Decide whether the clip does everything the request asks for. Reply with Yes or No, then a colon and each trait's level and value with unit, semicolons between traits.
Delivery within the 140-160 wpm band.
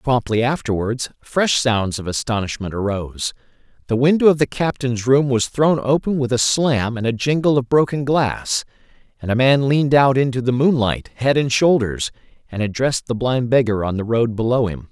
No: average, 185 wpm